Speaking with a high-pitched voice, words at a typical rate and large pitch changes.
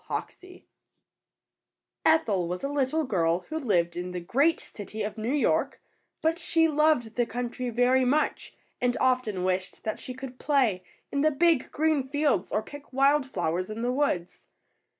Yes: very high, 255 Hz; average, 165 wpm; wide, 5.9 semitones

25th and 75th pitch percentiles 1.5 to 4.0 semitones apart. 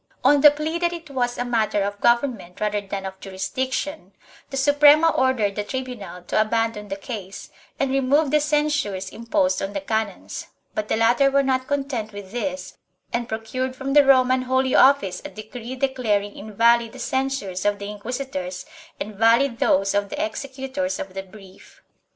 No: average, 5.0 semitones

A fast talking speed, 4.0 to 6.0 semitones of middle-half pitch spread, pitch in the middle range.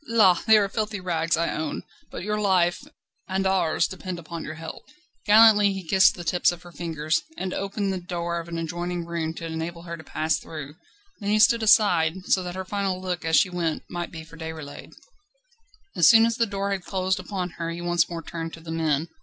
No: fast, 220 wpm; average, 2.9 semitones; medium, 175 Hz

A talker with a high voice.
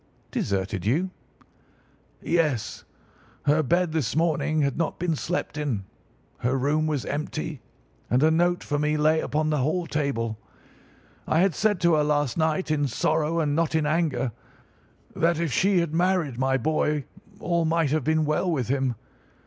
No: medium, 155 Hz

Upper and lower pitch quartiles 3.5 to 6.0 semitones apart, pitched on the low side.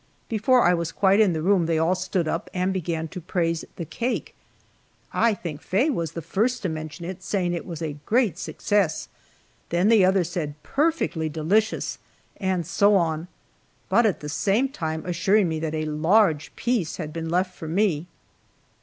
No: average, 4.0 semitones; medium, 175 Hz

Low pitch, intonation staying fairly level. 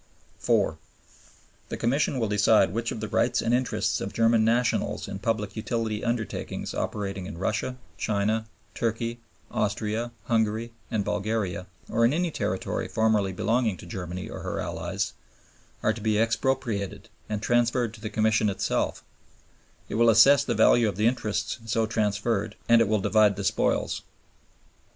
Yes: low, 110 Hz; narrow, 2.0 semitones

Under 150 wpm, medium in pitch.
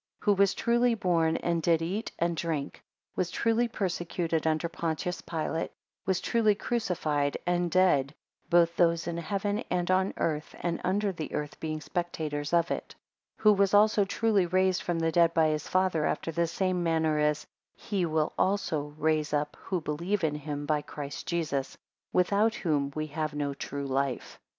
No: average, 180 wpm; medium, 170 Hz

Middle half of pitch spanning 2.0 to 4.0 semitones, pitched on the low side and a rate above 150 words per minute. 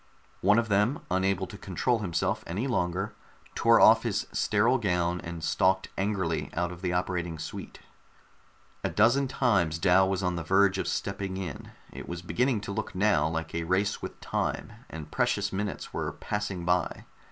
Yes: average, 2.8 semitones; very low, 95 Hz; average, 175 wpm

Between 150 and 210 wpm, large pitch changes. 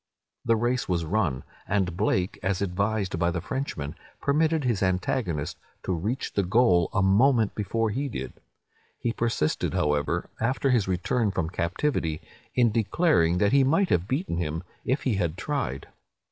Yes: average, 160 wpm; wide, 6.1 semitones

